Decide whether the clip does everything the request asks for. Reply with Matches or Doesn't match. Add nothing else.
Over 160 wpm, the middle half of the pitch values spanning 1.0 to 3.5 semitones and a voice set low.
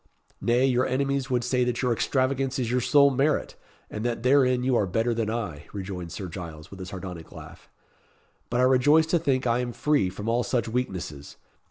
Doesn't match